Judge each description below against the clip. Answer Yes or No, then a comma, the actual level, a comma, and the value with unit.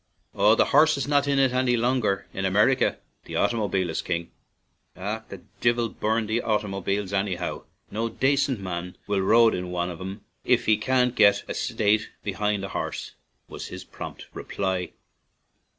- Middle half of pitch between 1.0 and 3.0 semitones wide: No, average, 3.7 semitones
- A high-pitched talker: No, low, 105 Hz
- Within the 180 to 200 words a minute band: No, average, 170 wpm